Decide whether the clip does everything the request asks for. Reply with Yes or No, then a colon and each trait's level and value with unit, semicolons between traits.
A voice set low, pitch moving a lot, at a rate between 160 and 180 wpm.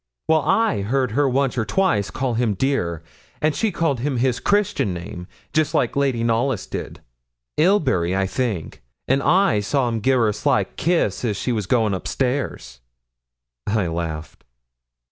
Yes: low, 120 Hz; wide, 5.7 semitones; average, 165 wpm